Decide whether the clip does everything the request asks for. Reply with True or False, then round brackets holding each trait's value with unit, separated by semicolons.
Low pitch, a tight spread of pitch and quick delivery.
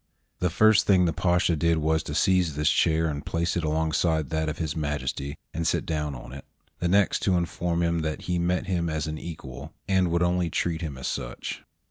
True (80 Hz; 2.2 semitones; 215 wpm)